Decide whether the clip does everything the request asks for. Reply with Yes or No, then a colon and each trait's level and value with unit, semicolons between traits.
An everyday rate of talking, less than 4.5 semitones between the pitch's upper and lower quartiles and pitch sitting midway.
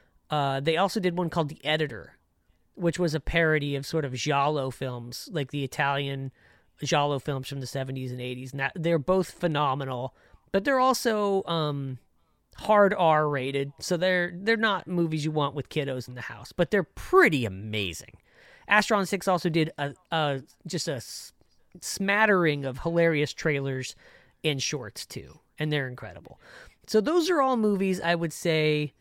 No: average, 165 wpm; average, 4.8 semitones; medium, 150 Hz